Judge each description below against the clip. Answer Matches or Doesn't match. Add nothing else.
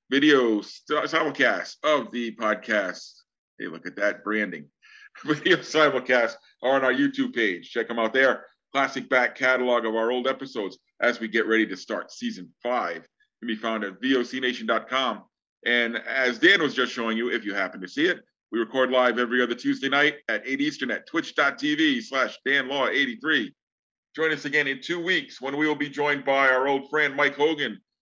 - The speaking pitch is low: Matches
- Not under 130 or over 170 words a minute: Doesn't match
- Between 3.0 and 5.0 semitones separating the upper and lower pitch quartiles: Matches